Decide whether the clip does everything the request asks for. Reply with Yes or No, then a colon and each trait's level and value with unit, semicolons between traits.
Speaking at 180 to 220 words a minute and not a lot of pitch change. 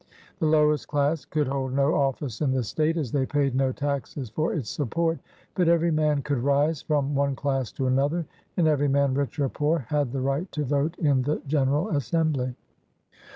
Yes: average, 195 wpm; narrow, 2.3 semitones